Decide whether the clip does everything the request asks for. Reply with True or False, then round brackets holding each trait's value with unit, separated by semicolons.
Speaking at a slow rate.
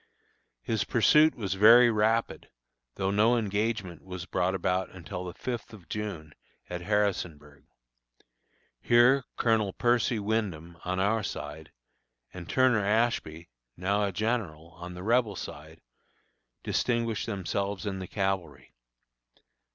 True (120 wpm)